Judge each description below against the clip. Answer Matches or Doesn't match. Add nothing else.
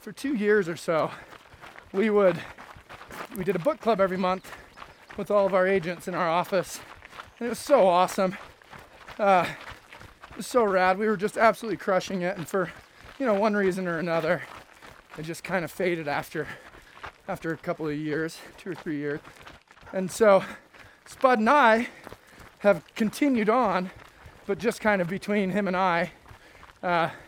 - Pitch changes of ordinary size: Matches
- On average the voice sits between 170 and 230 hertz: Matches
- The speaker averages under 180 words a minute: Matches